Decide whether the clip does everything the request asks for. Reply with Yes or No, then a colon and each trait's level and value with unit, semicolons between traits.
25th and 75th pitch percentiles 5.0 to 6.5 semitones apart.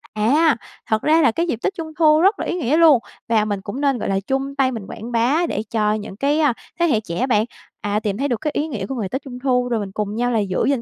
Yes: wide, 5.5 semitones